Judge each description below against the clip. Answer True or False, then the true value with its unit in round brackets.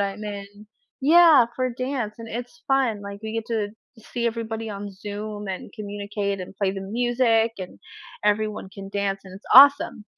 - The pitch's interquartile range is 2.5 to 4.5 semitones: True (2.8 semitones)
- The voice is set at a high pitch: True (215 Hz)